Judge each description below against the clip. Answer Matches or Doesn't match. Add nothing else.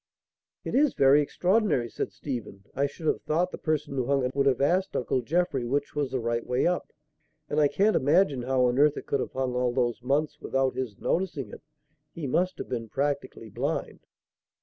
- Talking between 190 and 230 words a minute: Matches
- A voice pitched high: Doesn't match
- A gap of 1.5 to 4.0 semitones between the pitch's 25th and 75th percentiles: Matches